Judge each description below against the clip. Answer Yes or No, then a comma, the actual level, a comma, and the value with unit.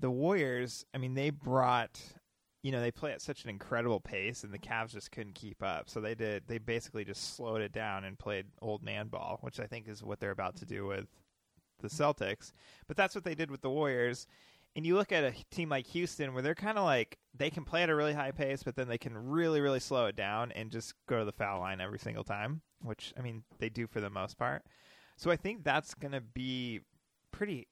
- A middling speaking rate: No, fast, 240 wpm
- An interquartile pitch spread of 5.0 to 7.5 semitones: Yes, average, 5.3 semitones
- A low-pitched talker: Yes, low, 125 Hz